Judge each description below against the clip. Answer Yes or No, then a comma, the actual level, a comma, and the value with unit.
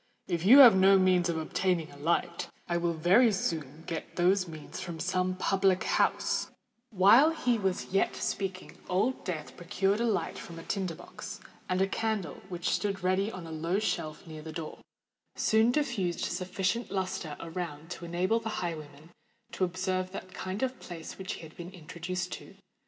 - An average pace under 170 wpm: No, average, 175 wpm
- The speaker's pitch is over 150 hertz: Yes, medium, 185 Hz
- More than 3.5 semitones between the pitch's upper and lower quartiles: No, narrow, 2.5 semitones